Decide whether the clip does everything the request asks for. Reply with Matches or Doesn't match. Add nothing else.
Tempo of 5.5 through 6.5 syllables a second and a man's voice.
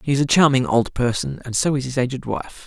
Matches